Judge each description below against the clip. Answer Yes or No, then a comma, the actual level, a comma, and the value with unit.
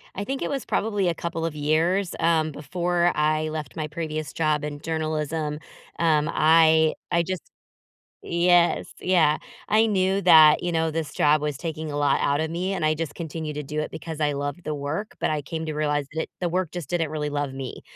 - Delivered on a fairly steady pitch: Yes, narrow, 2.3 semitones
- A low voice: No, medium, 160 Hz